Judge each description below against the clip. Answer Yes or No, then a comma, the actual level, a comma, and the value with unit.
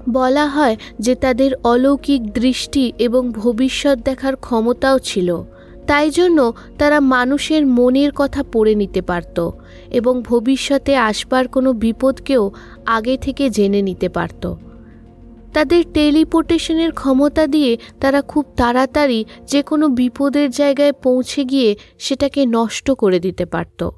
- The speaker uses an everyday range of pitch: Yes, average, 3.6 semitones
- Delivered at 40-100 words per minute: No, fast, 120 wpm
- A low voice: No, very high, 260 Hz